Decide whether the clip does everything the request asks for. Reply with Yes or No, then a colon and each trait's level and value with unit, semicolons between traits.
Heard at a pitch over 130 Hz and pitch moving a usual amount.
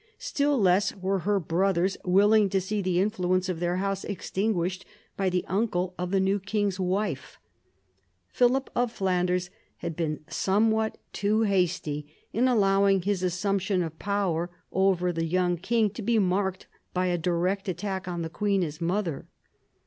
No: high, 190 Hz; narrow, 2.3 semitones